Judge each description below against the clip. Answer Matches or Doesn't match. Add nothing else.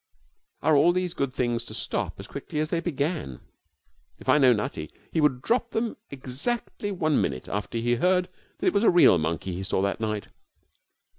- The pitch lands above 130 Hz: Matches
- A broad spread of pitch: Matches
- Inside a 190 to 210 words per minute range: Matches